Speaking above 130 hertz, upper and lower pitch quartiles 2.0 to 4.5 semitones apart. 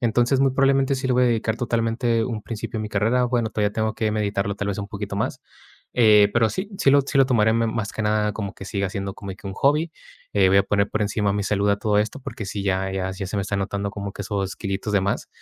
No: low, 105 Hz; average, 2.8 semitones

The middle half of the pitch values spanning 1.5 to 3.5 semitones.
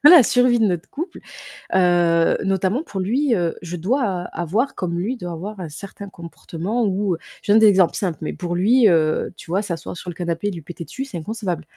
No: average, 4.1 semitones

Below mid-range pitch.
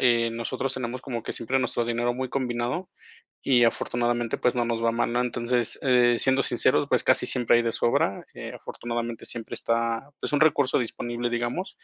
Yes: low, 120 Hz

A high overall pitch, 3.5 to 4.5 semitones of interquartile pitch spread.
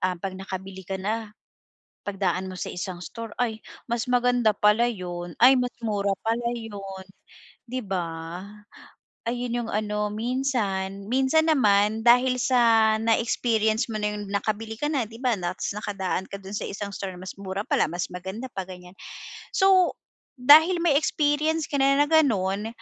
Yes: high, 220 Hz; average, 4.2 semitones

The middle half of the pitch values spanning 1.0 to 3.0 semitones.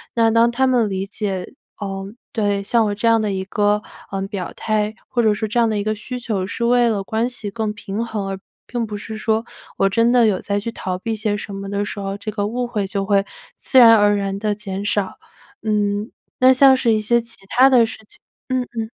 Yes: narrow, 2.5 semitones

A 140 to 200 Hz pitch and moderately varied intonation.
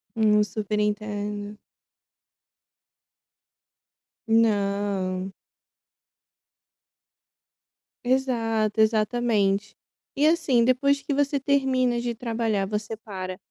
No: high, 220 Hz; average, 3.1 semitones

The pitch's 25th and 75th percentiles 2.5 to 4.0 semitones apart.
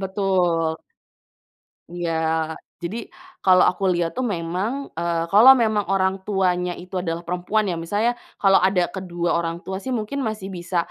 Yes: average, 2.9 semitones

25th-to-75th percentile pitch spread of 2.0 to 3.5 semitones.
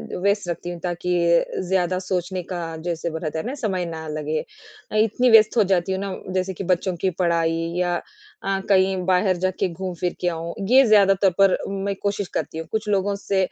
Yes: narrow, 2.4 semitones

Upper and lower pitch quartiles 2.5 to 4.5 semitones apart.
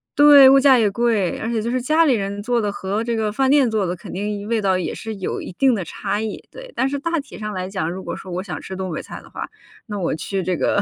No: average, 5.1 semitones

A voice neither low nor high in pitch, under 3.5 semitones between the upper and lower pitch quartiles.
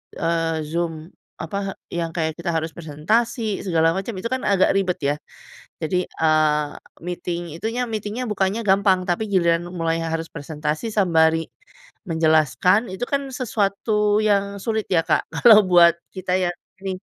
No: medium, 180 Hz; average, 4.0 semitones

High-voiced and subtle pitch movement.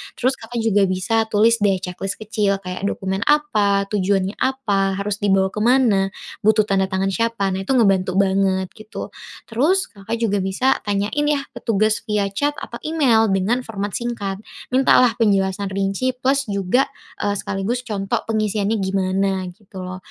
No: high, 205 Hz; average, 3.0 semitones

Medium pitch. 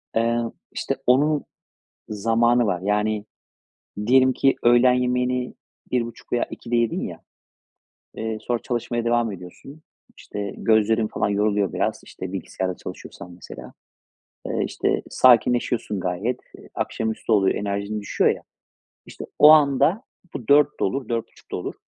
No: low, 115 Hz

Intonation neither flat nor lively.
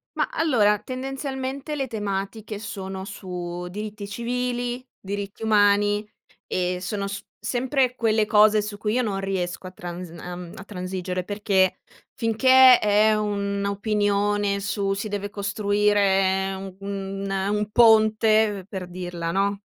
No: narrow, 2.1 semitones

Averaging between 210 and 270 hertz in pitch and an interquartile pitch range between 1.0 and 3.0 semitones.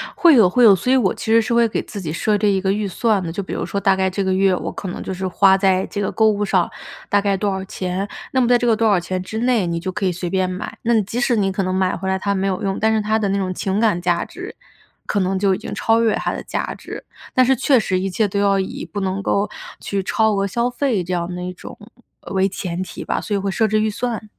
No: high, 195 Hz; average, 2.7 semitones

